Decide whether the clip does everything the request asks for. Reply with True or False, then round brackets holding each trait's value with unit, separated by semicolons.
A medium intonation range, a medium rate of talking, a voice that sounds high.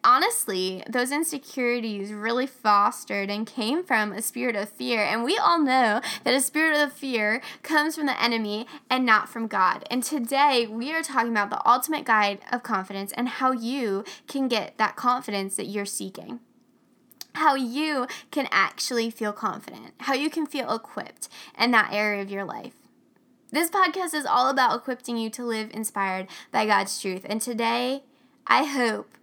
True (4.4 semitones; 170 wpm; 240 Hz)